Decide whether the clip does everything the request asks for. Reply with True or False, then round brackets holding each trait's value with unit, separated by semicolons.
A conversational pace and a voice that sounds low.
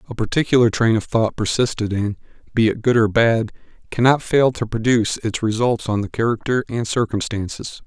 True (175 wpm; 115 Hz)